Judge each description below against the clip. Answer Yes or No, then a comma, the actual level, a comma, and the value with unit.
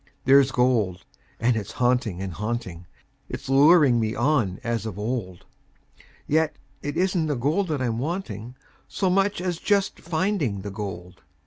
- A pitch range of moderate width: No, wide, 6.8 semitones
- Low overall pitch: Yes, low, 125 Hz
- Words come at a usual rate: Yes, average, 150 wpm